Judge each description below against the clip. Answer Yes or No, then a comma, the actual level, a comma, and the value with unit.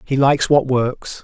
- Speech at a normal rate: Yes, average, 195 wpm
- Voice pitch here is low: Yes, low, 130 Hz